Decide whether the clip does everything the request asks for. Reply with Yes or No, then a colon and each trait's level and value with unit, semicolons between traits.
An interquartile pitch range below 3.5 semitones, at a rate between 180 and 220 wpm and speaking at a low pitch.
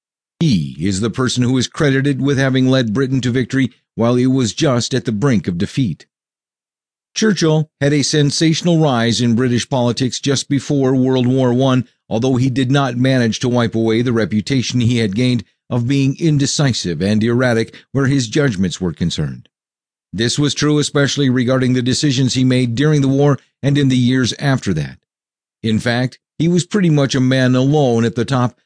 Yes: average, 2.7 semitones; average, 185 wpm; low, 130 Hz